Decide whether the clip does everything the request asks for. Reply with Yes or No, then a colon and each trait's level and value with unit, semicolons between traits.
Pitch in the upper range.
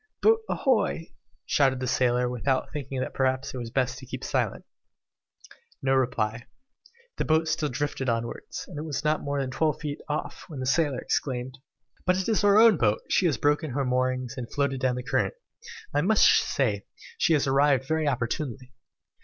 No: low, 135 Hz